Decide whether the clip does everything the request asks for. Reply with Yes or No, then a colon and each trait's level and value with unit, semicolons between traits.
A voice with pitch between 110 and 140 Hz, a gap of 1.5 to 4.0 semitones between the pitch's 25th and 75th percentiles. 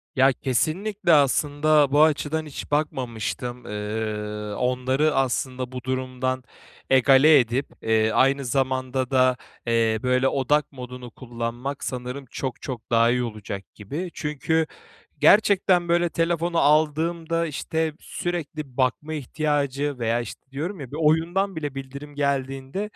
Yes: low, 135 Hz; average, 3.5 semitones